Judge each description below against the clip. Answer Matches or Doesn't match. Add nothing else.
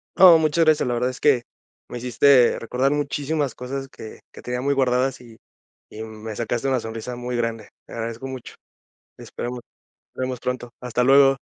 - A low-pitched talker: Matches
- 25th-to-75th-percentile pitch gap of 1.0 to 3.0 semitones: Matches